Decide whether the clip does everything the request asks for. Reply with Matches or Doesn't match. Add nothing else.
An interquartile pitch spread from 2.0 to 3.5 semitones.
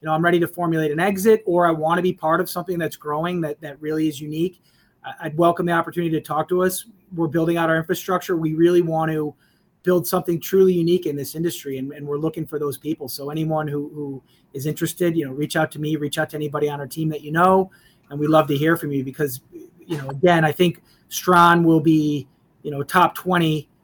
Matches